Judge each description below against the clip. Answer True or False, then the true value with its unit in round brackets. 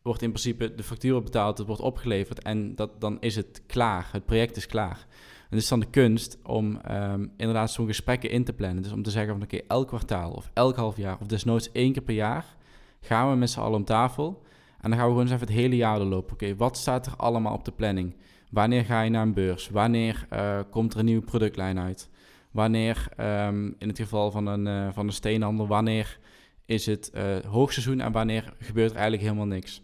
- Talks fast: True (235 wpm)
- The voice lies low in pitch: True (110 Hz)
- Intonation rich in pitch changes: False (2.5 semitones)